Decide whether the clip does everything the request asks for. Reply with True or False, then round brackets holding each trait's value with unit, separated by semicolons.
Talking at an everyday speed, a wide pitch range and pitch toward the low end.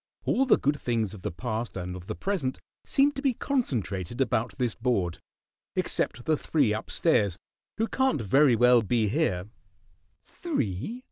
True (160 wpm; 7.5 semitones; 120 Hz)